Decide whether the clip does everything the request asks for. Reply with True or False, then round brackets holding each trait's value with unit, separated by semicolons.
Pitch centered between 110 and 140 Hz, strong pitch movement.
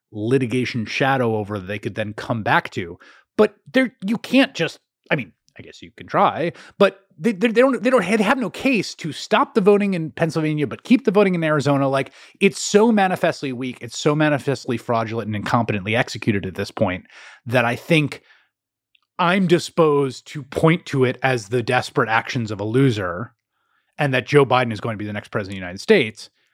True (135 Hz; 8.5 semitones)